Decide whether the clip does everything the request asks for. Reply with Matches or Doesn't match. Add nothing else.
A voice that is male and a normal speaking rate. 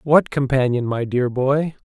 Matches